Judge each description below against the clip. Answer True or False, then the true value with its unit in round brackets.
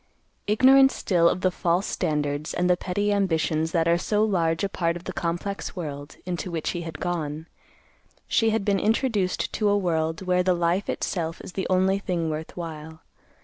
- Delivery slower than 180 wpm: False (190 wpm)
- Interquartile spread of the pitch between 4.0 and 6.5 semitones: False (3.2 semitones)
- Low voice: False (175 Hz)